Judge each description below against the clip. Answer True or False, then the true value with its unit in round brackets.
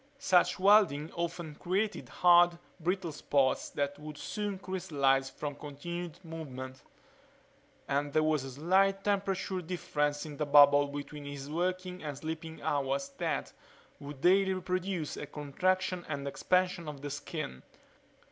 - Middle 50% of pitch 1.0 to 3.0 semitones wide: False (4.2 semitones)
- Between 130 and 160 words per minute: True (135 wpm)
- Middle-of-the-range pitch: True (155 Hz)